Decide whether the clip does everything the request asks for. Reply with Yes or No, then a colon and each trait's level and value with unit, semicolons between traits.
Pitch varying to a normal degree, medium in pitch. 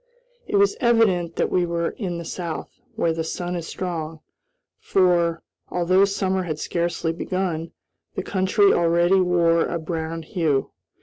No: narrow, 2.0 semitones; medium, 175 Hz